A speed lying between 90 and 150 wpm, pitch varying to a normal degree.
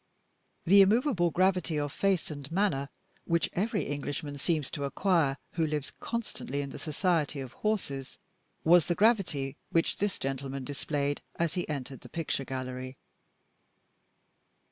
Yes: average, 140 wpm; average, 4.8 semitones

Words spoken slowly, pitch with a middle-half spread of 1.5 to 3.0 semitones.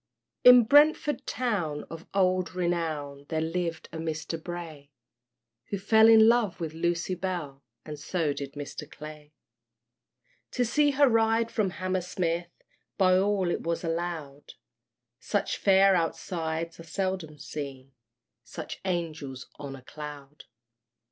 No: slow, 130 wpm; average, 4.1 semitones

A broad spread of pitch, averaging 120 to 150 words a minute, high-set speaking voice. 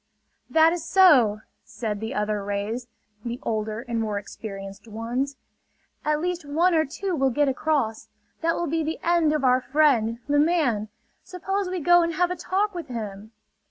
No: wide, 7.2 semitones; average, 175 wpm; very high, 280 Hz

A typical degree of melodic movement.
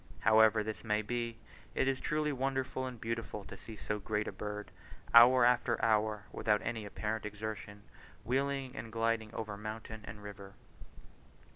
No: narrow, 2.3 semitones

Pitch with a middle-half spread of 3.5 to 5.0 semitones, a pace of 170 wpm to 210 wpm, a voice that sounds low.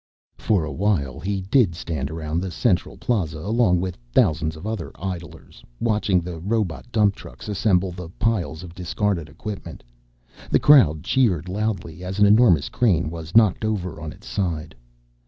No: average, 4.4 semitones; average, 160 wpm; very low, 90 Hz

